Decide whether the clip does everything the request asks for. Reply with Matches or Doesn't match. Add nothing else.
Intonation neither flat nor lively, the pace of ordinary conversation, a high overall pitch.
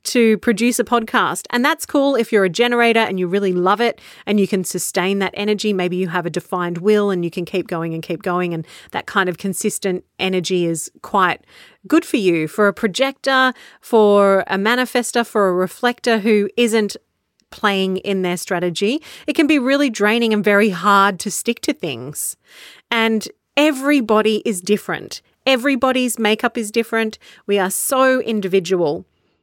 Matches